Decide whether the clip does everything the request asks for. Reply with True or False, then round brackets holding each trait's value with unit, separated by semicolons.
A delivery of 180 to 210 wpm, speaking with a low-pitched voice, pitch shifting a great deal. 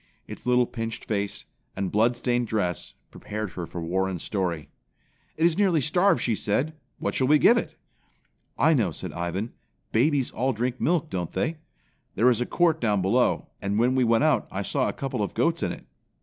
True (190 wpm; 120 Hz; 5.9 semitones)